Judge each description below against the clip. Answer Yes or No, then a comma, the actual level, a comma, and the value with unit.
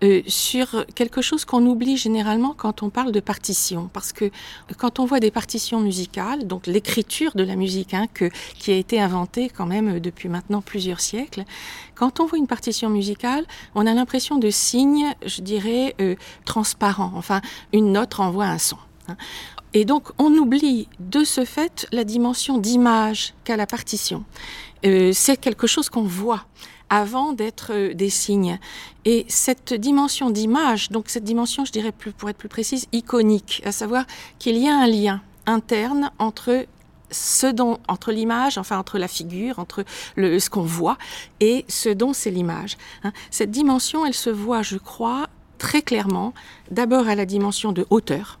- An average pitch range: Yes, average, 3.8 semitones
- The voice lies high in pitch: Yes, high, 220 Hz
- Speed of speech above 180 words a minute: No, average, 170 wpm